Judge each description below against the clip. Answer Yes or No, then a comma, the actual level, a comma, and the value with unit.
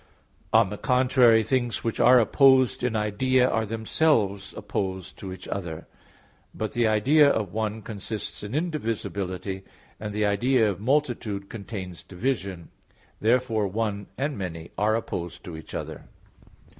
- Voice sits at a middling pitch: No, low, 110 Hz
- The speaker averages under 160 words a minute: Yes, average, 140 wpm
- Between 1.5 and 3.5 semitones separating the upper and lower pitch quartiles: No, average, 4.0 semitones